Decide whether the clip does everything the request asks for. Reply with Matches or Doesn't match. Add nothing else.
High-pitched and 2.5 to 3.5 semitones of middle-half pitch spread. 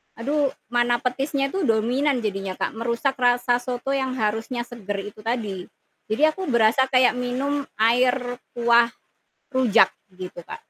Matches